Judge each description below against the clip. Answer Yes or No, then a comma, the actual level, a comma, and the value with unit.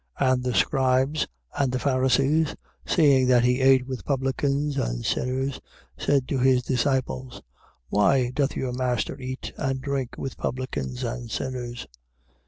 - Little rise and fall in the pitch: Yes, narrow, 1.4 semitones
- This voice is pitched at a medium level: No, low, 130 Hz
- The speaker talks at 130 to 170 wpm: Yes, average, 145 wpm